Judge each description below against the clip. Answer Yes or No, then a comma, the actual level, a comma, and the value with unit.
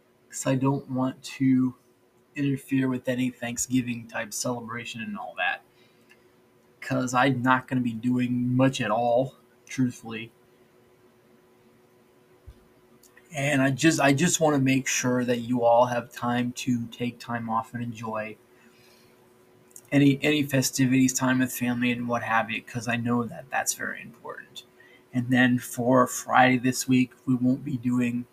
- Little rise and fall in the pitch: Yes, narrow, 1.0 semitones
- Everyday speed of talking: Yes, average, 155 wpm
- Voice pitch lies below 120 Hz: No, low, 125 Hz